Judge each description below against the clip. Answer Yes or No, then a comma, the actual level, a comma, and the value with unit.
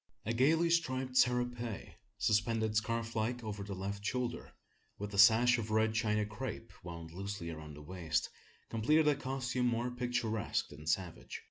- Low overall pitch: Yes, low, 110 Hz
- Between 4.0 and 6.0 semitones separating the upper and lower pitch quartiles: No, average, 3.5 semitones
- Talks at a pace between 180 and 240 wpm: No, average, 155 wpm